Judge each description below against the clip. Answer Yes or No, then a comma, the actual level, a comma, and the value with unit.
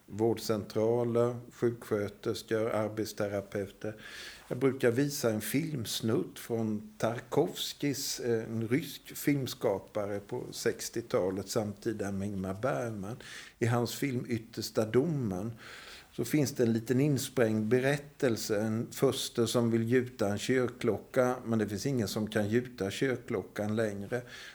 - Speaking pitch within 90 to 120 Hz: Yes, low, 115 Hz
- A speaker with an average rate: No, slow, 115 wpm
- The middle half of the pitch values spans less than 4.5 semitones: Yes, average, 2.8 semitones